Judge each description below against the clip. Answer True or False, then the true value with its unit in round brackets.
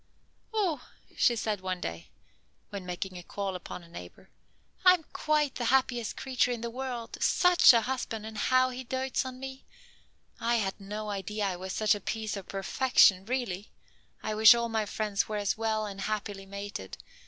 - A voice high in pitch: True (215 Hz)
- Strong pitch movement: False (4.2 semitones)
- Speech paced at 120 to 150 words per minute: False (180 wpm)